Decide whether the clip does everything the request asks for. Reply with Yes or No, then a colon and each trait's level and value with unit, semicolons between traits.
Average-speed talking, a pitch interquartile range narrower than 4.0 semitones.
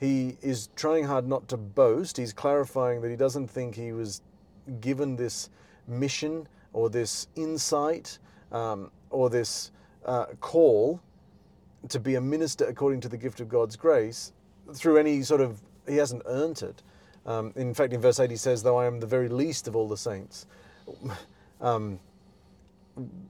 Yes: average, 165 wpm; average, 3.5 semitones